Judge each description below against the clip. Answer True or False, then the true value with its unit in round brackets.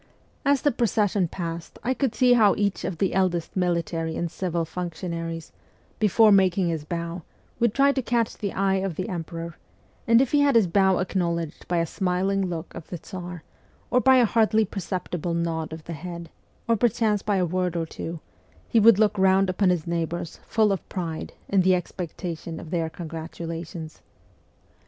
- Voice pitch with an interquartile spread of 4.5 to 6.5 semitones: False (3.6 semitones)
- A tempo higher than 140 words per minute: True (180 wpm)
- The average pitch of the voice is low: False (180 Hz)